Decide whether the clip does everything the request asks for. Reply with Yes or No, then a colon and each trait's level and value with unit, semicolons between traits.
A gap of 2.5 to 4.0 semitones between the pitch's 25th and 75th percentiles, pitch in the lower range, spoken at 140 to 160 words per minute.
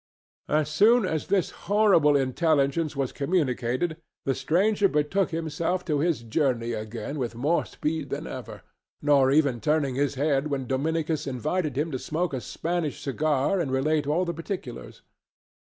No: average, 3.6 semitones; medium, 150 Hz; average, 150 wpm